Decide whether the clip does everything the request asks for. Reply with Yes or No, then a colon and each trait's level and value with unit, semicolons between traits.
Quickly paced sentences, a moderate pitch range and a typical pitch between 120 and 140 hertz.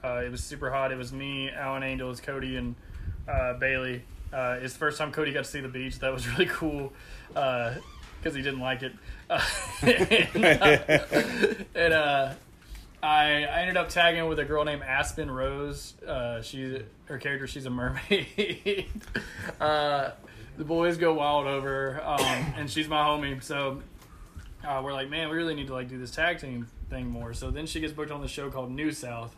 No: average, 195 wpm; average, 3.0 semitones; low, 135 Hz